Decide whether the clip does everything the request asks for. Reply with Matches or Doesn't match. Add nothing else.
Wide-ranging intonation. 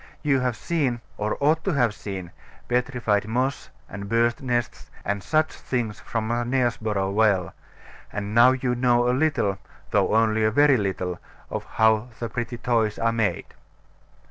Doesn't match